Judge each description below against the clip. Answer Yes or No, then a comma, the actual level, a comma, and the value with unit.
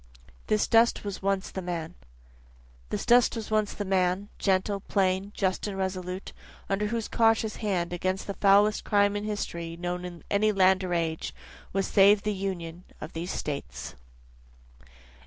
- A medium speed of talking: Yes, average, 155 wpm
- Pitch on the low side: No, high, 195 Hz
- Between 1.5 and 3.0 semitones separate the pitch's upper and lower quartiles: Yes, narrow, 2.4 semitones